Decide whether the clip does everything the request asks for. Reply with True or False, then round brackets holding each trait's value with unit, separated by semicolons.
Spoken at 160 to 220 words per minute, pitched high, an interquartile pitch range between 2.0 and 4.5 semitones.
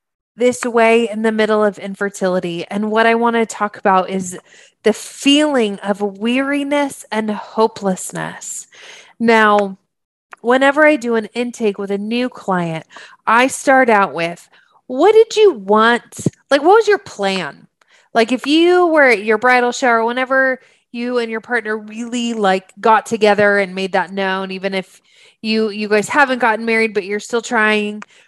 True (165 wpm; 225 Hz; 3.5 semitones)